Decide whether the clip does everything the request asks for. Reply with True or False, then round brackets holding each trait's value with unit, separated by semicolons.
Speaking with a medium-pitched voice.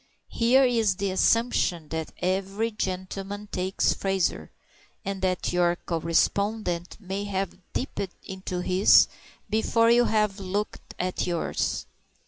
False (195 Hz)